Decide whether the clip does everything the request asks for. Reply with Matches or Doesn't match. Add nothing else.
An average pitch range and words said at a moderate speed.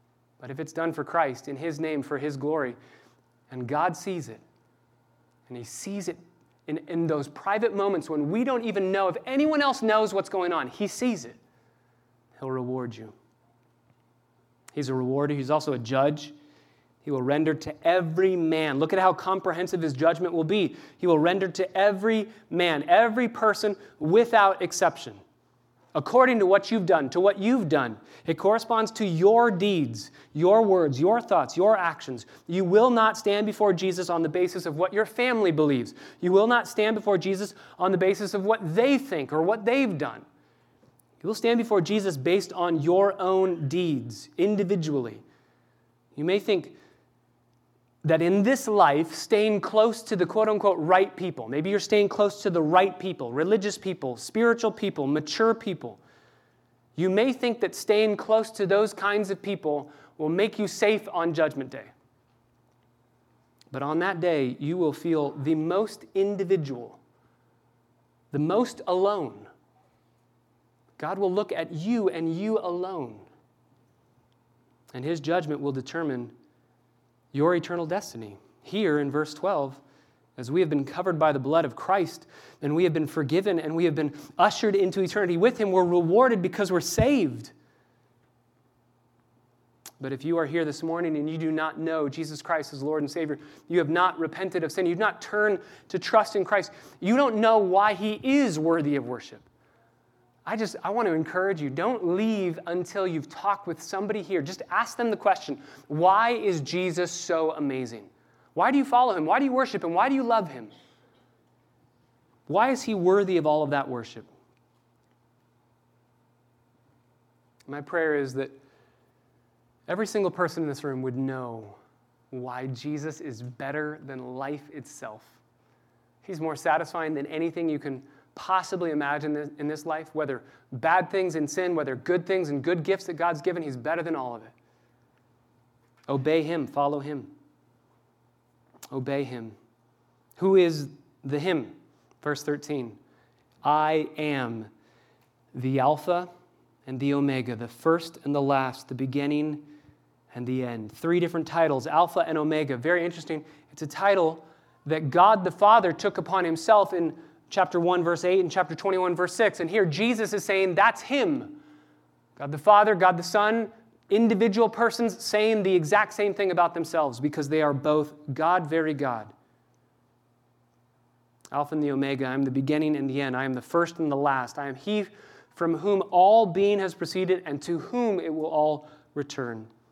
Doesn't match